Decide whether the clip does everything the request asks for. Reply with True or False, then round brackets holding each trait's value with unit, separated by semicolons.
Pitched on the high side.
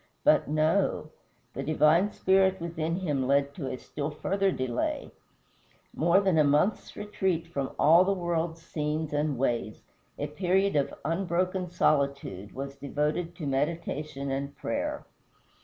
False (155 Hz)